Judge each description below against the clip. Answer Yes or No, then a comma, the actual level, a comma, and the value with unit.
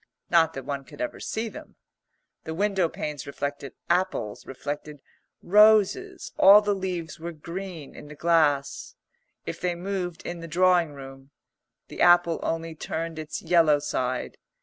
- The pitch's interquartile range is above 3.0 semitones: Yes, average, 4.0 semitones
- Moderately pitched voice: Yes, medium, 165 Hz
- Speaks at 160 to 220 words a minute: No, average, 150 wpm